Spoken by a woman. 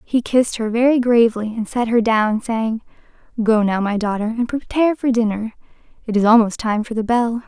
Yes: female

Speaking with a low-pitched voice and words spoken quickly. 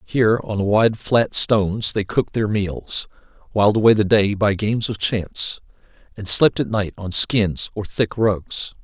No: low, 105 Hz; average, 175 wpm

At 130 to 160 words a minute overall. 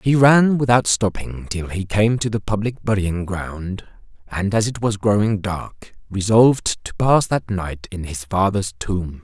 No: average, 175 wpm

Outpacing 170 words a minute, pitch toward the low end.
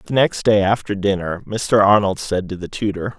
Yes: fast, 205 wpm; low, 100 Hz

